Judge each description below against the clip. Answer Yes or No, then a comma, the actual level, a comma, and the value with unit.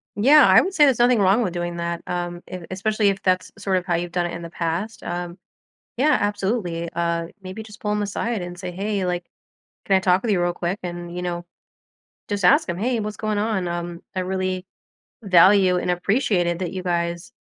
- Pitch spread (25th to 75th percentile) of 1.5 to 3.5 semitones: Yes, average, 3.0 semitones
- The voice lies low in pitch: No, medium, 185 Hz